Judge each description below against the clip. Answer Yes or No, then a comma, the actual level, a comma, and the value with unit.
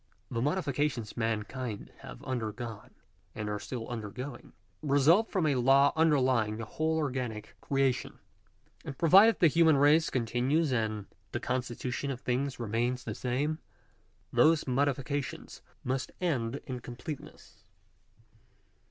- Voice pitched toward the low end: Yes, low, 130 Hz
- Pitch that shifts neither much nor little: Yes, average, 3.6 semitones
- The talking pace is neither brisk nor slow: No, slow, 125 wpm